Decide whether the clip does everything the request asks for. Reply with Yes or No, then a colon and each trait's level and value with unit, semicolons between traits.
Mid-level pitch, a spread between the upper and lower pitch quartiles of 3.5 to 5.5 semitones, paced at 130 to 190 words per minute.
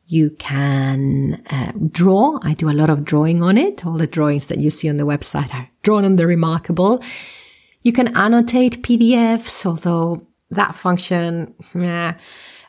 Yes: medium, 170 Hz; average, 4.6 semitones; average, 160 wpm